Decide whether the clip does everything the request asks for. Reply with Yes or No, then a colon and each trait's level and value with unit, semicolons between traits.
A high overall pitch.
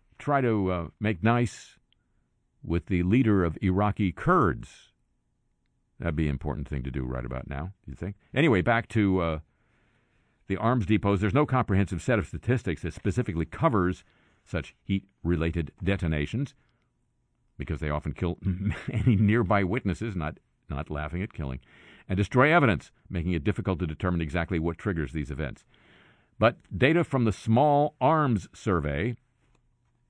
No: very low, 95 Hz